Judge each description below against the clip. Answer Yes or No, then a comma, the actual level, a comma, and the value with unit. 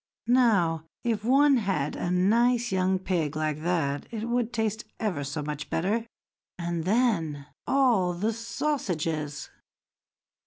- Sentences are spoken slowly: Yes, slow, 125 wpm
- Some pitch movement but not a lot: No, wide, 6.5 semitones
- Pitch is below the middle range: No, high, 190 Hz